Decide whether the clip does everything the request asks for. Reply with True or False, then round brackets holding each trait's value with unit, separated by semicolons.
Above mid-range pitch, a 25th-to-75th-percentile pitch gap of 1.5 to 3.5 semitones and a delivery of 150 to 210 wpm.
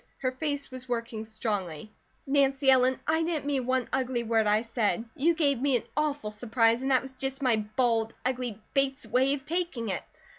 True (255 Hz; 3.2 semitones; 190 wpm)